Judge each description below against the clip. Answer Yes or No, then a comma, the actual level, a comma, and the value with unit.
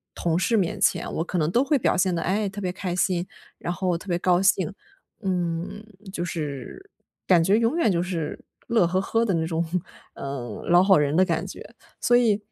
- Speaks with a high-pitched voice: No, medium, 180 Hz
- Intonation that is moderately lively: Yes, average, 3.3 semitones